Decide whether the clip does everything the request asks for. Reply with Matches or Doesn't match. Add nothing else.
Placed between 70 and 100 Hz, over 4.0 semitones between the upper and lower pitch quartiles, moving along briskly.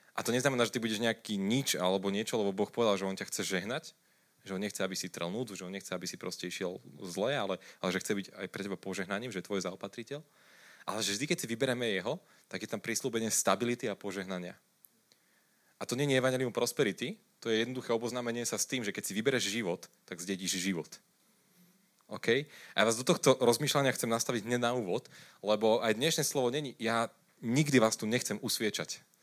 Doesn't match